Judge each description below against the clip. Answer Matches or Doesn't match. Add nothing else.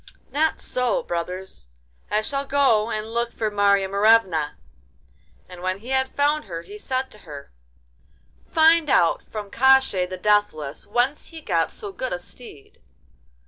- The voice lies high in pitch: Matches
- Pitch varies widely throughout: Matches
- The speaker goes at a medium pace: Matches